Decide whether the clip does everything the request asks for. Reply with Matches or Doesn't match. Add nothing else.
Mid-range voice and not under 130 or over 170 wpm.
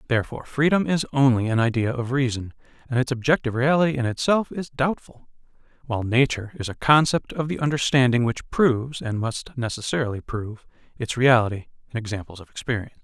Doesn't match